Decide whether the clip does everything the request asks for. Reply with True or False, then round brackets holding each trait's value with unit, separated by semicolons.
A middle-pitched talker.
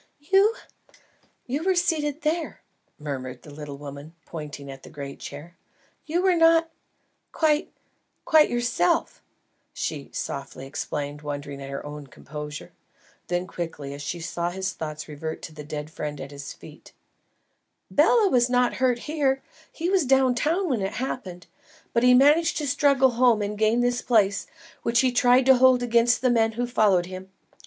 False (225 Hz)